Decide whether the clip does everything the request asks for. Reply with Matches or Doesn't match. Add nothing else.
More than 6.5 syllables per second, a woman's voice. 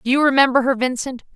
Matches